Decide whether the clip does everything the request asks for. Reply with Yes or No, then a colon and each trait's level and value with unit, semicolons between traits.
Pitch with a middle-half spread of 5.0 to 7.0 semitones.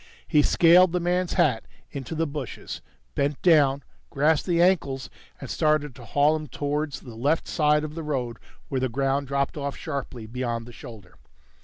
No: average, 3.1 semitones